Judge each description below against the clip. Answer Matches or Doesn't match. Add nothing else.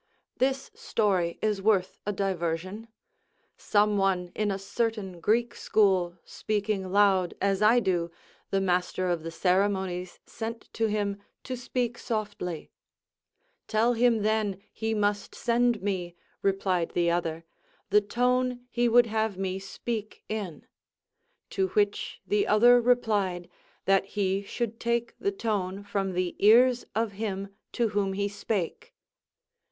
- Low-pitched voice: Doesn't match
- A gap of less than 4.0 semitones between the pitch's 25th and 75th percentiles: Matches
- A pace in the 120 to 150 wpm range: Matches